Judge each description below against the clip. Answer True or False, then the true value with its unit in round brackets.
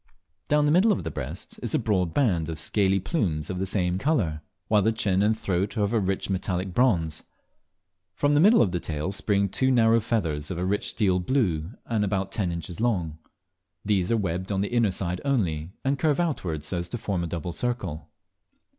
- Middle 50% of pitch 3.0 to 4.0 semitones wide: False (4.7 semitones)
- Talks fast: True (210 wpm)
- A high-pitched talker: False (95 Hz)